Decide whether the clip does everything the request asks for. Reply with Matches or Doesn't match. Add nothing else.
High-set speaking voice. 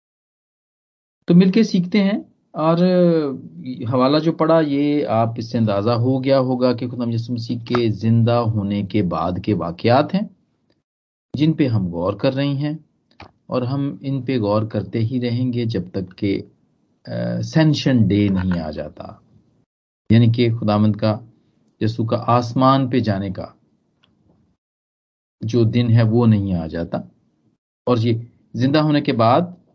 Doesn't match